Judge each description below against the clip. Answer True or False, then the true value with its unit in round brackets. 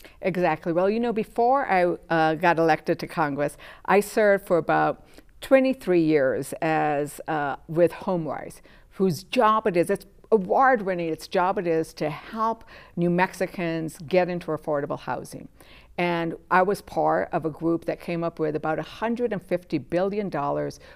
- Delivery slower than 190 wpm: True (155 wpm)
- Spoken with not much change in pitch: False (3.4 semitones)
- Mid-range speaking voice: True (175 Hz)